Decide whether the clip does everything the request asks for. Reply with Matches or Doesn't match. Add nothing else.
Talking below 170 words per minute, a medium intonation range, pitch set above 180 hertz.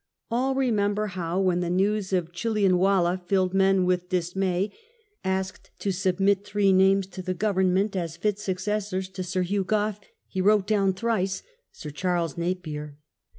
Doesn't match